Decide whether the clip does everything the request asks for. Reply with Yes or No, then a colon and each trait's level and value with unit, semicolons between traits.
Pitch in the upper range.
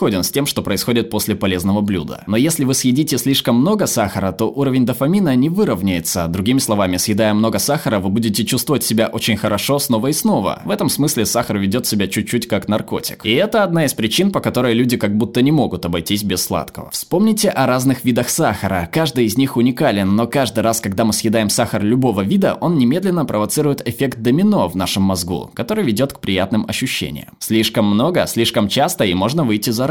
No: low, 115 Hz